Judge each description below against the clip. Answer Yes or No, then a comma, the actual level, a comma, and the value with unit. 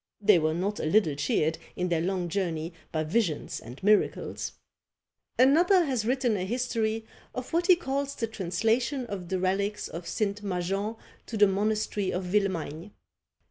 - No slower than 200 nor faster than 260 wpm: No, average, 160 wpm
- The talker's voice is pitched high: Yes, high, 200 Hz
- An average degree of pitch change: Yes, average, 4.3 semitones